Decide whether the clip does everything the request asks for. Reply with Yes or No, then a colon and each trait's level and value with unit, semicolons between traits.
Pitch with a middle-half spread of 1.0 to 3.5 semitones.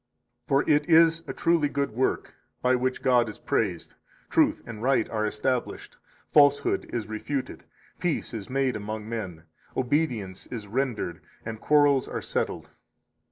No: average, 4.7 semitones